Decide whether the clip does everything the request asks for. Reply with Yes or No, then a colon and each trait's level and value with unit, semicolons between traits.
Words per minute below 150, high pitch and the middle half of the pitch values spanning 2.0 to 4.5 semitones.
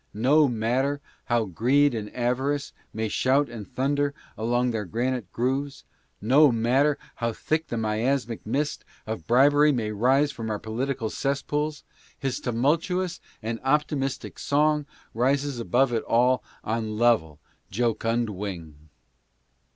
No: slow, 135 wpm; low, 125 Hz; average, 4.0 semitones